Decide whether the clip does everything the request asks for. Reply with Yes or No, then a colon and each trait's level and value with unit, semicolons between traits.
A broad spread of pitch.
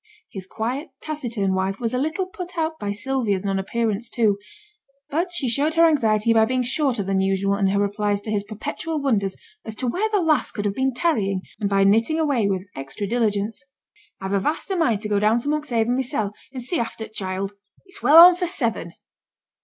Yes: wide, 6.6 semitones